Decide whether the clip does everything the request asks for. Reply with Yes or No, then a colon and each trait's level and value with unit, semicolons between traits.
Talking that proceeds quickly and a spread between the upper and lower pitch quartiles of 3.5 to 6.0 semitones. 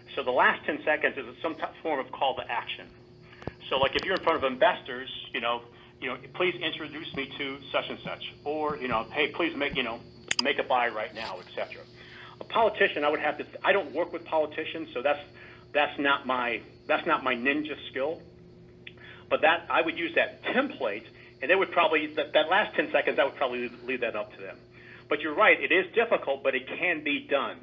Yes: fast, 225 wpm; average, 4.0 semitones